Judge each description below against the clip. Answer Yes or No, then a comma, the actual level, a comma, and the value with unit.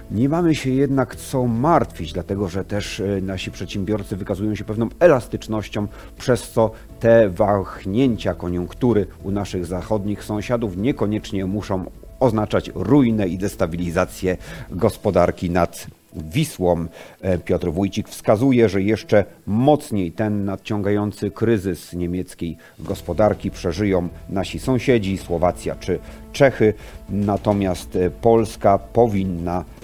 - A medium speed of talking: No, slow, 105 wpm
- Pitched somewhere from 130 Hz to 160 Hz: No, low, 100 Hz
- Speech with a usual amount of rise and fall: Yes, average, 3.5 semitones